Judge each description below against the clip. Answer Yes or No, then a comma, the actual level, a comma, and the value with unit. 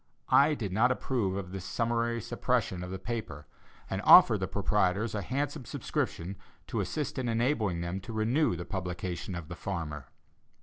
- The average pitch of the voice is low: Yes, low, 100 Hz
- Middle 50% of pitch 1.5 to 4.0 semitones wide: No, average, 4.7 semitones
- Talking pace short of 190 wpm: Yes, average, 170 wpm